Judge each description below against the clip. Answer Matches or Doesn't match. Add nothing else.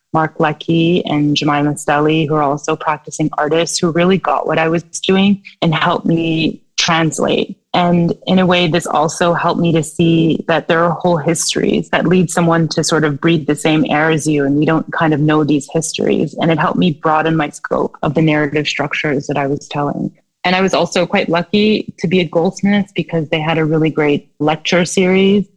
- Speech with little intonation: Matches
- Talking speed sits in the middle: Doesn't match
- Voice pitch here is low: Doesn't match